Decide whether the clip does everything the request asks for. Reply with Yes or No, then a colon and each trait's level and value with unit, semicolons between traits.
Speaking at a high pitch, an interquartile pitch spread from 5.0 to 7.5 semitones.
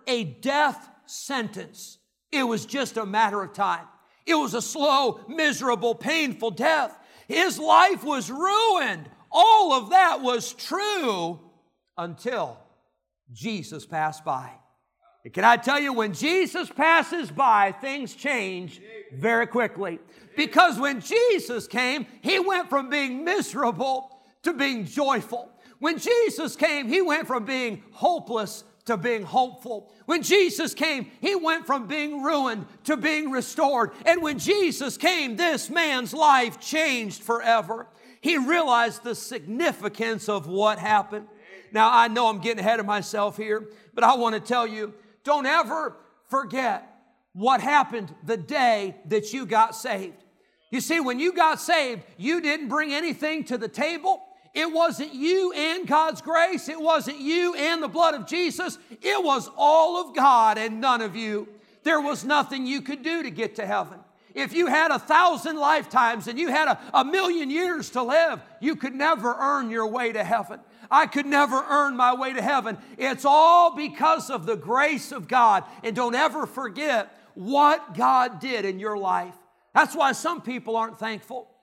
Yes: very high, 265 Hz; wide, 5.5 semitones